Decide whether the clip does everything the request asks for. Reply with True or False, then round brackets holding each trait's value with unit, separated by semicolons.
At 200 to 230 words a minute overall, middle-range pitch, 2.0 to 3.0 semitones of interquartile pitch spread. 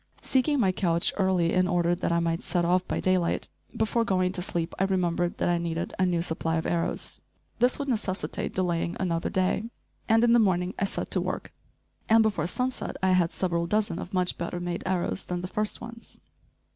True (205 wpm; 180 Hz; 2.6 semitones)